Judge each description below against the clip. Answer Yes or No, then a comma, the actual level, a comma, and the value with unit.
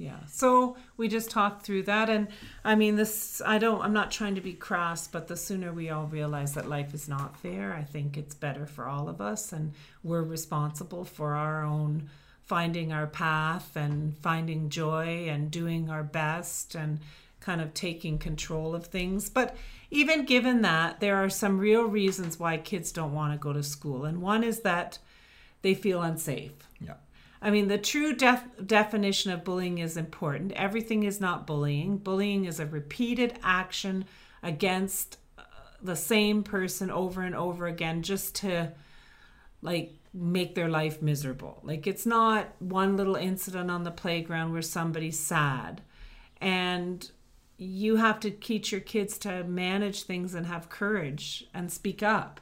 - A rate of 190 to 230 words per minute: No, average, 170 wpm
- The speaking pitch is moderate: Yes, medium, 175 Hz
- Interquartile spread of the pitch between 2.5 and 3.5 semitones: No, average, 4.3 semitones